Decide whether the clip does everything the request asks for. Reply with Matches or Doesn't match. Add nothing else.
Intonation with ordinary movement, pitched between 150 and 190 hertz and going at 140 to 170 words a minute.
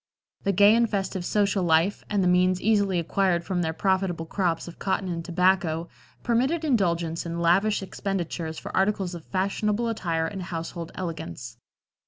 Matches